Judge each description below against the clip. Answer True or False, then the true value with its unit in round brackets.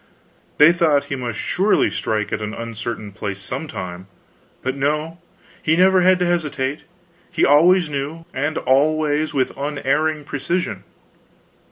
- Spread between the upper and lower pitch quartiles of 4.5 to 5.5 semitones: False (3.8 semitones)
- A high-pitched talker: False (145 Hz)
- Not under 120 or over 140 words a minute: True (135 wpm)